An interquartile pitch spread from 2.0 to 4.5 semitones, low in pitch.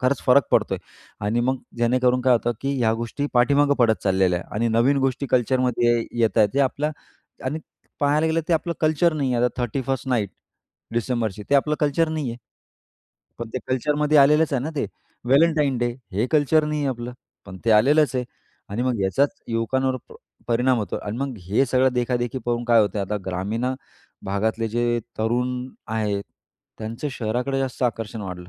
Yes: average, 3.4 semitones; low, 125 Hz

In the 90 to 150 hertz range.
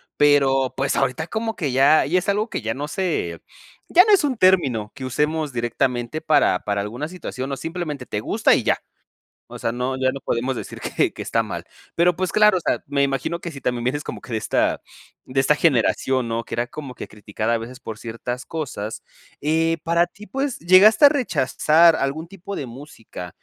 Yes: medium, 140 Hz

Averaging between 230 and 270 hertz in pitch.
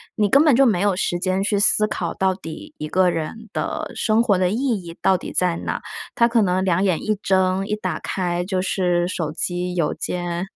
No: medium, 185 Hz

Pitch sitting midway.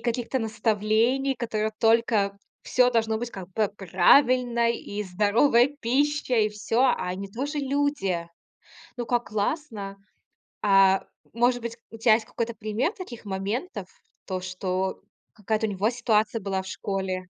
No: high, 220 Hz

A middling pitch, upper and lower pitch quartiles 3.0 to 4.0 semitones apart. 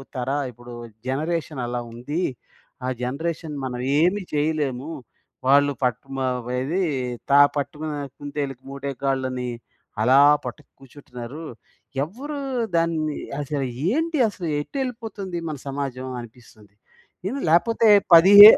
No: medium, 145 Hz; average, 4.6 semitones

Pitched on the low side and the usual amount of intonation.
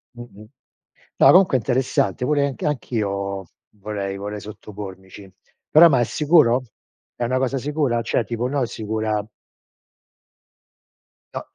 Yes: low, 115 Hz; average, 4.4 semitones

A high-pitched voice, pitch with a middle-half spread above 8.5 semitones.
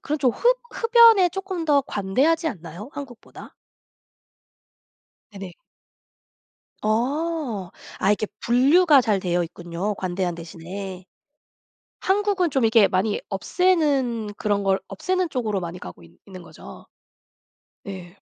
Yes: high, 220 Hz; wide, 8.9 semitones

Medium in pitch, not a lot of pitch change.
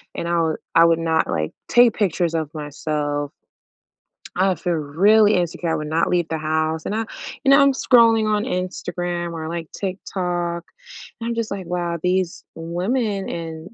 No: medium, 175 Hz; average, 3.5 semitones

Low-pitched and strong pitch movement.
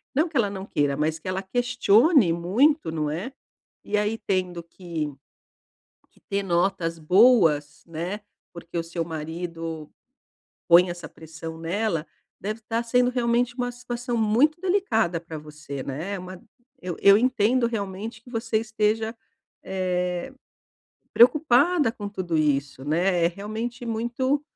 No: high, 195 Hz; wide, 6.0 semitones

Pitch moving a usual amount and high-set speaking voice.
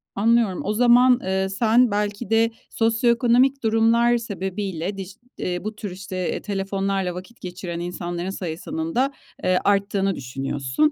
Yes: average, 4.0 semitones; high, 200 Hz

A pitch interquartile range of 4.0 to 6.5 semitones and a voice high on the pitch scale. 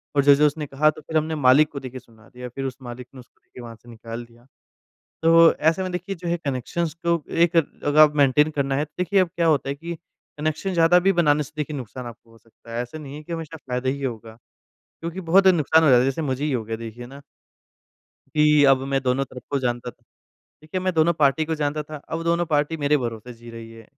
No: average, 4.4 semitones; medium, 145 Hz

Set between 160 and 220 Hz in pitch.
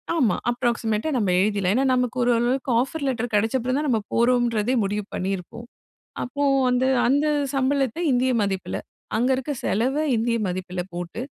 No: high, 240 Hz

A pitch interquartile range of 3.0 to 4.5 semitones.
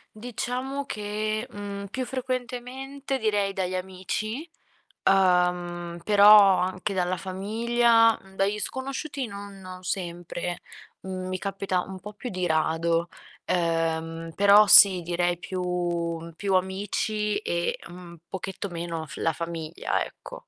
Yes: average, 3.5 semitones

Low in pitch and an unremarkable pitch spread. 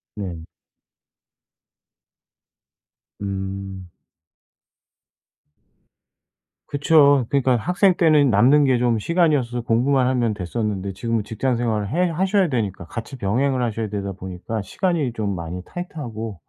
No: low, 115 Hz; wide, 6.0 semitones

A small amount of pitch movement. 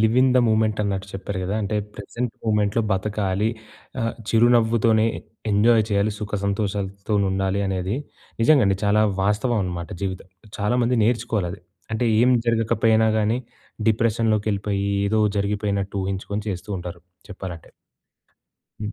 Yes: narrow, 2.2 semitones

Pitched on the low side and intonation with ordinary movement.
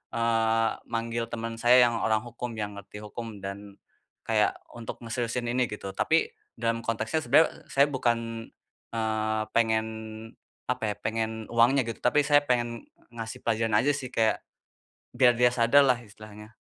No: low, 115 Hz; narrow, 1.7 semitones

